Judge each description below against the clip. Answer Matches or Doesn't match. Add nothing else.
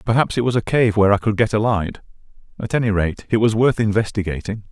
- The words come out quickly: Matches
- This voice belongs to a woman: Doesn't match